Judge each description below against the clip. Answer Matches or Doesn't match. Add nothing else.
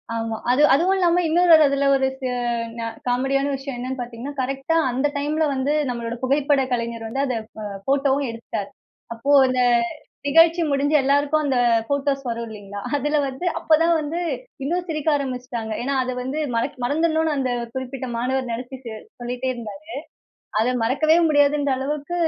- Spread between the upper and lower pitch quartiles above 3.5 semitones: Doesn't match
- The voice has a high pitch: Matches